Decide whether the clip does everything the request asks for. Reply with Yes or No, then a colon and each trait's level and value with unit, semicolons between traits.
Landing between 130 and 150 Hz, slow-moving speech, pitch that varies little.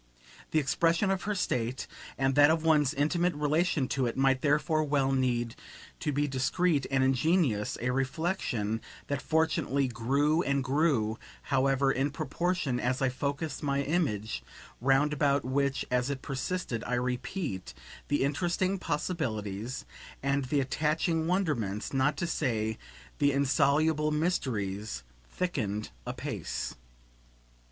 No: medium, 140 Hz; slow, 130 wpm; average, 3.7 semitones